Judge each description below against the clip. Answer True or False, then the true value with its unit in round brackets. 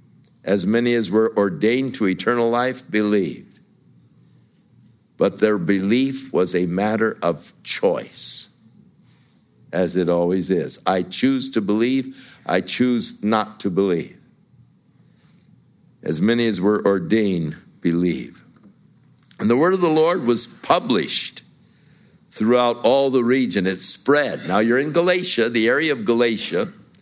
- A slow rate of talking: True (130 wpm)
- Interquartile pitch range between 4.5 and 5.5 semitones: False (4.0 semitones)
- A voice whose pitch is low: True (110 Hz)